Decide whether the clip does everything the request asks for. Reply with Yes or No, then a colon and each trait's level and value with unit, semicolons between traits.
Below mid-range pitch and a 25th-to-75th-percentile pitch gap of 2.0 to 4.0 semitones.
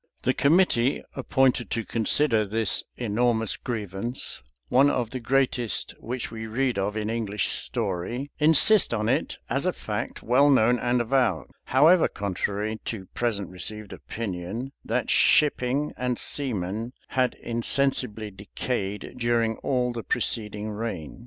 Yes: low, 115 Hz; average, 3.4 semitones